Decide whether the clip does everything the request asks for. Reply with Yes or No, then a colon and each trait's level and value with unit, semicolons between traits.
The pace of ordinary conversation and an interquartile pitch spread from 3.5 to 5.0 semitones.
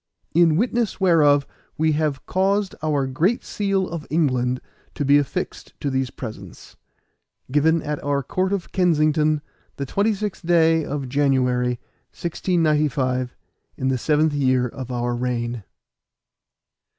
No: slow, 125 wpm; average, 4.6 semitones